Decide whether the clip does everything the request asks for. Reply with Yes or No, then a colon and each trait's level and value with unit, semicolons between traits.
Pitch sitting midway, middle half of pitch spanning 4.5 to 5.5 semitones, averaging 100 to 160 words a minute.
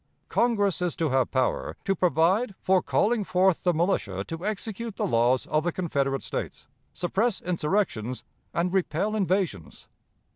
Yes: medium, 180 Hz; average, 4.9 semitones; average, 145 wpm